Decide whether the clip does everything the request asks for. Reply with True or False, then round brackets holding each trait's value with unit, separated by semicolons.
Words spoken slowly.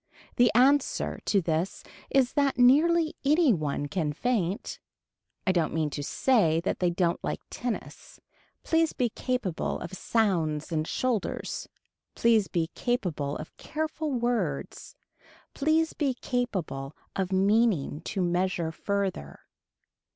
True (125 wpm)